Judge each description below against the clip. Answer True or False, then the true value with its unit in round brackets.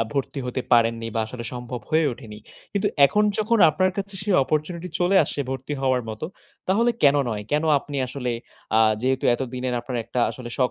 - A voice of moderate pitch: False (130 Hz)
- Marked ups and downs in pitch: True (5.8 semitones)